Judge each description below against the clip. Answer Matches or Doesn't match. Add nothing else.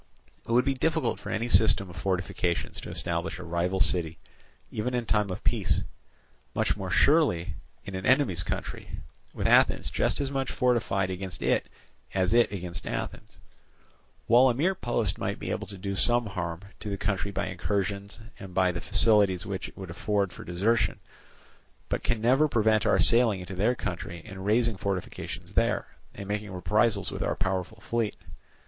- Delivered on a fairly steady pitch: Doesn't match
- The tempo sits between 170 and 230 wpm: Matches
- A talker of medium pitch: Doesn't match